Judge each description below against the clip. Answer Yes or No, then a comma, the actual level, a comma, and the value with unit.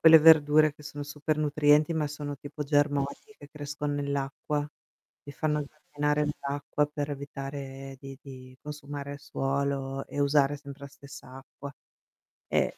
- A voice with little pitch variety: Yes, narrow, 1.1 semitones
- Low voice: No, medium, 145 Hz